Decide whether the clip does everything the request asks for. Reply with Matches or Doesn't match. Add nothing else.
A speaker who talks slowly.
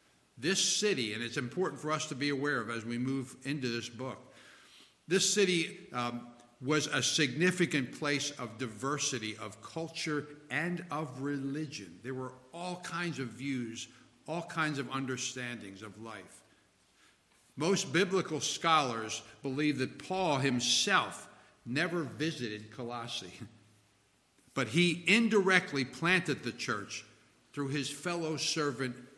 Matches